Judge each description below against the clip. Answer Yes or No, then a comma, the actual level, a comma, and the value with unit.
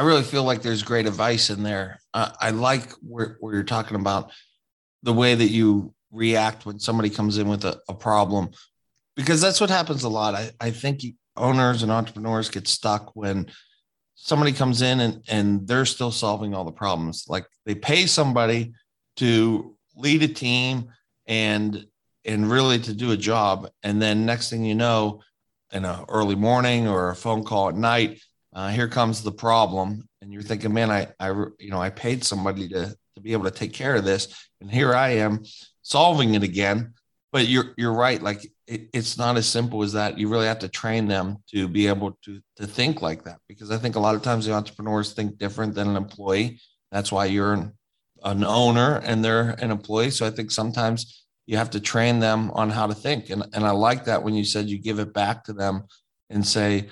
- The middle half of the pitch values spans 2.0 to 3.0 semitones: Yes, narrow, 2.4 semitones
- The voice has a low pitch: Yes, low, 110 Hz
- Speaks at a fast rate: Yes, fast, 210 wpm